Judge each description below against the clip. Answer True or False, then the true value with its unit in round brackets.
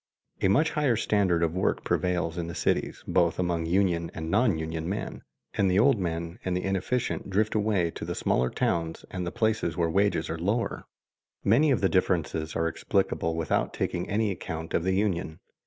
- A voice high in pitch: False (90 Hz)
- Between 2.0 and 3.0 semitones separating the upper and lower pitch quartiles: False (3.7 semitones)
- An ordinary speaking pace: True (190 wpm)